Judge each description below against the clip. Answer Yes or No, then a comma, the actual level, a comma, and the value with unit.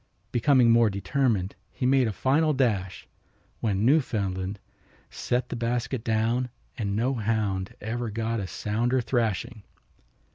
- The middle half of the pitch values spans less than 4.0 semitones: Yes, average, 3.2 semitones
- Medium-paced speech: No, slow, 130 wpm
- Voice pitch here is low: Yes, low, 115 Hz